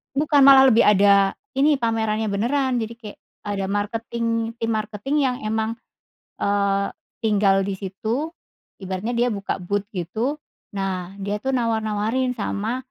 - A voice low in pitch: No, high, 220 Hz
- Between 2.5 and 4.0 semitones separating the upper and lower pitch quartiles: Yes, average, 3.1 semitones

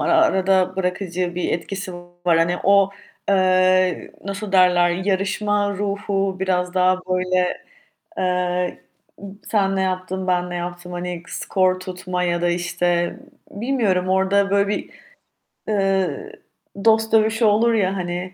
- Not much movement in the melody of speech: Yes, narrow, 1.8 semitones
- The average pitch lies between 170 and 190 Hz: Yes, medium, 185 Hz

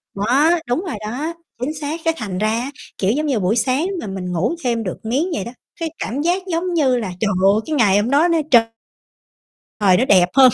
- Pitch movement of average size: No, wide, 6.7 semitones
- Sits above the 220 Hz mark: Yes, very high, 250 Hz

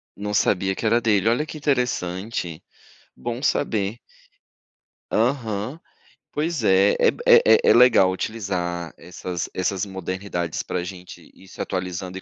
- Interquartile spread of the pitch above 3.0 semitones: Yes, average, 4.1 semitones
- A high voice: No, low, 100 Hz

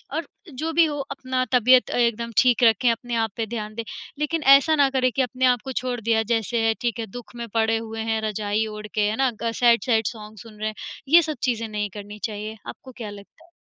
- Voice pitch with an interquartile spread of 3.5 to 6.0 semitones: No, average, 2.8 semitones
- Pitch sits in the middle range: No, high, 230 Hz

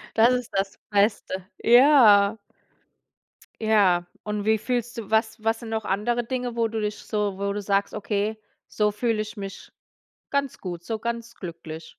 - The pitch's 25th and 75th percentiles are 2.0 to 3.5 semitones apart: Yes, narrow, 2.5 semitones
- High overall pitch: Yes, high, 215 Hz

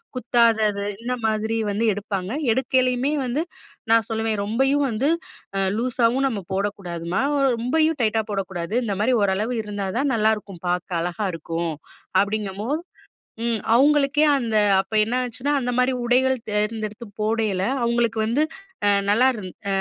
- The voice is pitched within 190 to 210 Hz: No, high, 220 Hz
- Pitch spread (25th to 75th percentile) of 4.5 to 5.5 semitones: No, average, 3.7 semitones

